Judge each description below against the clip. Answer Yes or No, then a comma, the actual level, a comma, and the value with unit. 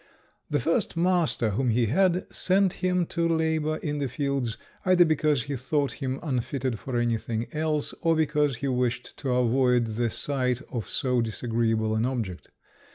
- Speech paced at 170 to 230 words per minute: No, average, 160 wpm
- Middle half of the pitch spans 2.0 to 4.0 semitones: No, average, 4.8 semitones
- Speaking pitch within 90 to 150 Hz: Yes, low, 135 Hz